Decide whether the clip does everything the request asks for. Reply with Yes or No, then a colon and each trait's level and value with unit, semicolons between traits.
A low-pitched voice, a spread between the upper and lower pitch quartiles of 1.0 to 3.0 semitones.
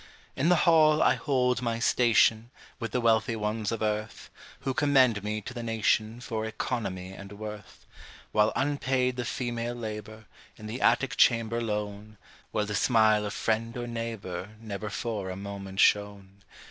Yes: low, 110 Hz; narrow, 2.4 semitones